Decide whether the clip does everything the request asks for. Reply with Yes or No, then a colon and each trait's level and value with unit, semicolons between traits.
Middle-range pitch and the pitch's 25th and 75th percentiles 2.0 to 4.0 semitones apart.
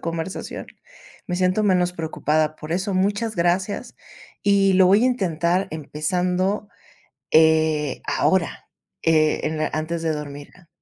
Yes: medium, 175 Hz; average, 3.3 semitones